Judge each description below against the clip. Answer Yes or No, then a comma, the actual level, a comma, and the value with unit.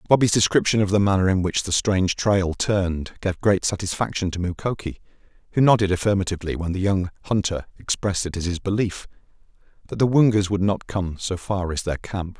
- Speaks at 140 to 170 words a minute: No, average, 190 wpm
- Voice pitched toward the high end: No, very low, 95 Hz